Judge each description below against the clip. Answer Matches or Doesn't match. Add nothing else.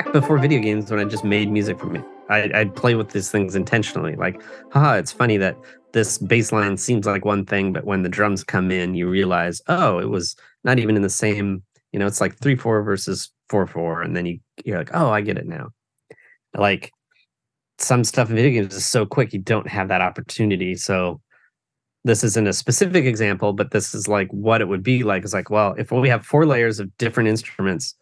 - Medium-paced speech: Doesn't match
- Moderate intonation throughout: Matches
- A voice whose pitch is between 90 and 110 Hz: Matches